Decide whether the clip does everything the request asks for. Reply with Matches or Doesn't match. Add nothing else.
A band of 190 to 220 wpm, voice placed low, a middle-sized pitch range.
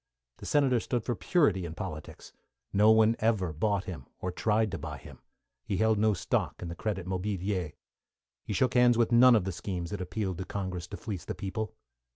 Matches